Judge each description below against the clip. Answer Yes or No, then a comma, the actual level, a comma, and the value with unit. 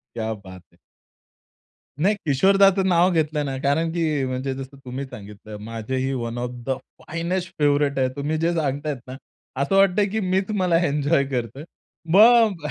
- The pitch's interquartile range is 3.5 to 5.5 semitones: Yes, average, 5.2 semitones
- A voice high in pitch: No, medium, 145 Hz